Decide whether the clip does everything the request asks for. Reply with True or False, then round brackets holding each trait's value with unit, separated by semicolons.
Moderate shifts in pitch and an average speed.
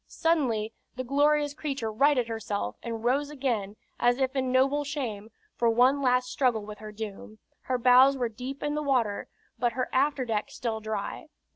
True (3.8 semitones; 170 wpm)